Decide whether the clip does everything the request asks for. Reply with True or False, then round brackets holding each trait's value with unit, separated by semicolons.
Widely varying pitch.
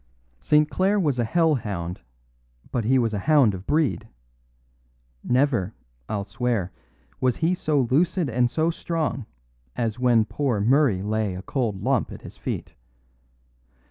True (5.7 semitones)